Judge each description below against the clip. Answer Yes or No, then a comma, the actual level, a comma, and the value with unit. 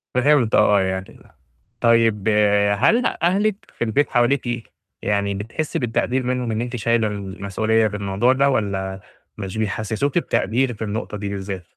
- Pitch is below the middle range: Yes, low, 110 Hz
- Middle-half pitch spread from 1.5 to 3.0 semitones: No, average, 3.8 semitones